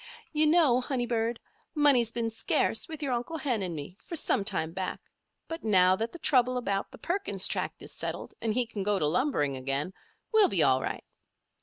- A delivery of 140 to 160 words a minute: No, average, 200 wpm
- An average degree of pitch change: No, wide, 7.1 semitones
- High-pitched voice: Yes, high, 230 Hz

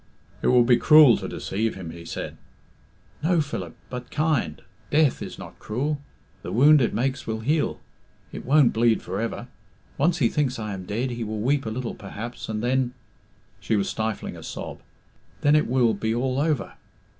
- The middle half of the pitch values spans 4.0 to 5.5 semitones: Yes, average, 4.5 semitones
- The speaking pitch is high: No, low, 120 Hz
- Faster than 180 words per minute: Yes, average, 190 wpm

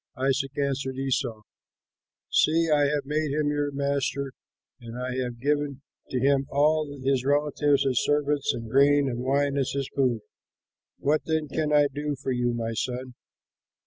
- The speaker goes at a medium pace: Yes, average, 160 wpm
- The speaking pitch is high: No, medium, 140 Hz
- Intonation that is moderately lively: No, narrow, 2.1 semitones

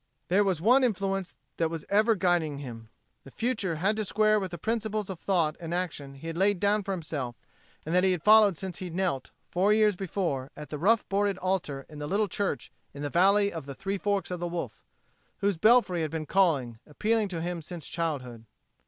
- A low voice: No, medium, 180 Hz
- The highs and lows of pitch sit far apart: No, average, 4.3 semitones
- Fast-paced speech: Yes, fast, 215 wpm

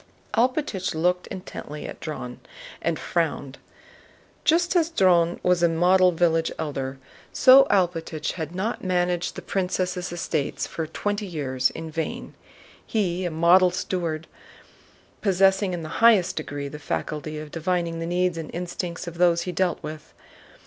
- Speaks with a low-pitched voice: No, medium, 175 Hz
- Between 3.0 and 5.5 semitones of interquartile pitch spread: No, narrow, 2.6 semitones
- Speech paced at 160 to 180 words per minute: No, average, 150 wpm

